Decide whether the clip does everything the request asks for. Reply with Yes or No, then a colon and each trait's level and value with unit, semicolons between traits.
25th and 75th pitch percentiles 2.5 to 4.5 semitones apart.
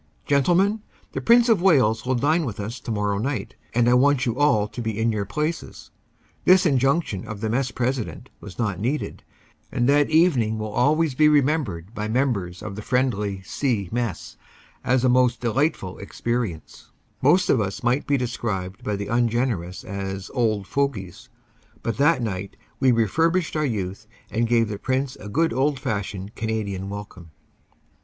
No: average, 5.2 semitones